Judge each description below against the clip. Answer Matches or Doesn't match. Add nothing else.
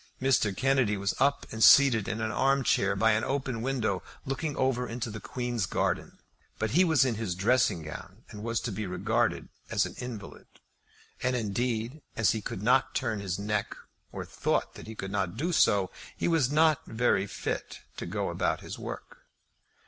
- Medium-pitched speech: Doesn't match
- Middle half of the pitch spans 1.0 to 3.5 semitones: Doesn't match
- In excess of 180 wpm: Matches